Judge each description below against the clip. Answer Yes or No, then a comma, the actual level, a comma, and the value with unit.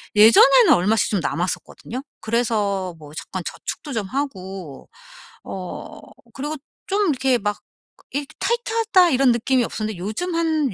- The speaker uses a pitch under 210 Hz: No, high, 235 Hz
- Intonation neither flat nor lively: No, wide, 6.8 semitones